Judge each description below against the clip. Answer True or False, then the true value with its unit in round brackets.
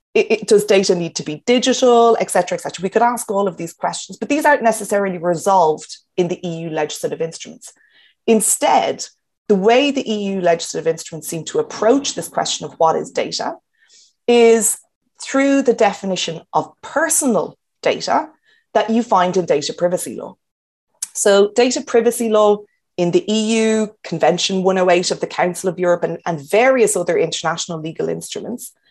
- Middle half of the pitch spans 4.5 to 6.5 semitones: True (5.0 semitones)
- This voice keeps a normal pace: True (165 wpm)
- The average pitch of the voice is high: True (205 Hz)